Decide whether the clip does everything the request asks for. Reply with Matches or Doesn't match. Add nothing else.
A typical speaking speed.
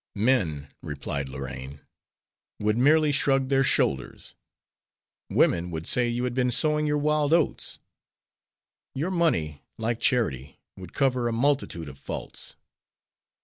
Doesn't match